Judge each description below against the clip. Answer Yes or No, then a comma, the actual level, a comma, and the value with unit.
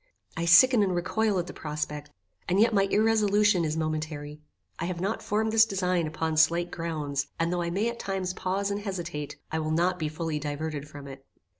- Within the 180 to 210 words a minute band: Yes, average, 200 wpm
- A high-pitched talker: No, medium, 170 Hz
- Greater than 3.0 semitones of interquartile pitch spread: Yes, average, 4.2 semitones